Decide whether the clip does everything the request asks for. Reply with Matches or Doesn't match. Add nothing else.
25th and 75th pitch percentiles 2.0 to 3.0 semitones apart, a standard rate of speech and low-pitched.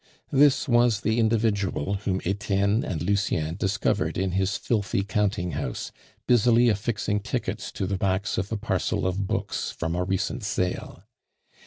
Matches